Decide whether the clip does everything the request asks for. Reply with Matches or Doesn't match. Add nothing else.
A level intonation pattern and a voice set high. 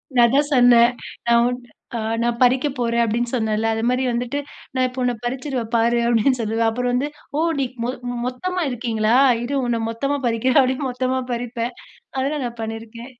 Matches